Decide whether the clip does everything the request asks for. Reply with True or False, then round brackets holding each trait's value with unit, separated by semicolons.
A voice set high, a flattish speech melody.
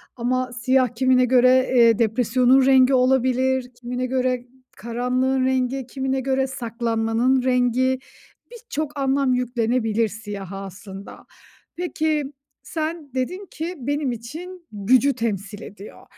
True (255 Hz; 2.1 semitones)